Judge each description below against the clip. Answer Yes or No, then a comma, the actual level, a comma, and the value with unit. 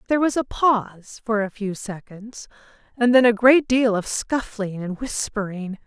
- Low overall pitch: No, high, 220 Hz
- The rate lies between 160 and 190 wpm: Yes, average, 175 wpm